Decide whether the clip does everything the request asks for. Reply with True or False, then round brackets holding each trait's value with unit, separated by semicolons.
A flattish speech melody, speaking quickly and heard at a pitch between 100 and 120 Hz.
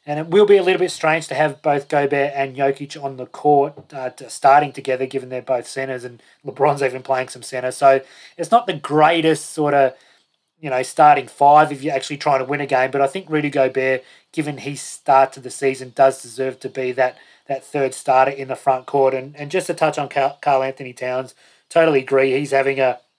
False (2.1 semitones; 225 wpm; 135 Hz)